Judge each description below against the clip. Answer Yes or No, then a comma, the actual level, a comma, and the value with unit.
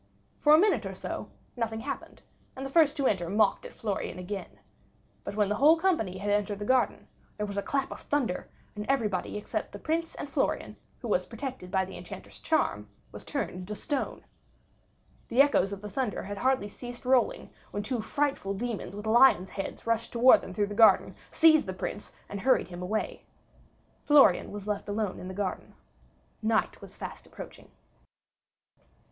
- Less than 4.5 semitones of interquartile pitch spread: No, average, 5.1 semitones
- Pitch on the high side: Yes, high, 215 Hz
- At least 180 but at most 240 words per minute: Yes, average, 185 wpm